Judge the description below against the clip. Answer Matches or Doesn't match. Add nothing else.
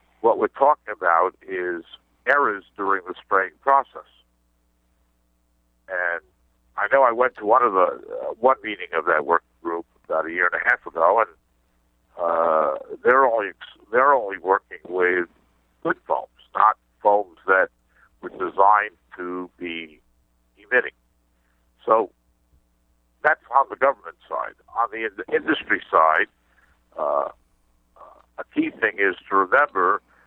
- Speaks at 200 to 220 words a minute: Doesn't match